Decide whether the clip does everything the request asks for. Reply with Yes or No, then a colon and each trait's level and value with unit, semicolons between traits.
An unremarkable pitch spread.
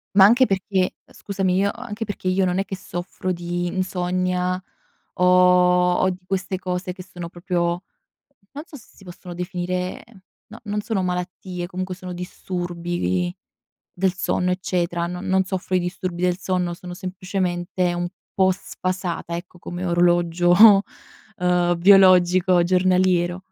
No: narrow, 1.2 semitones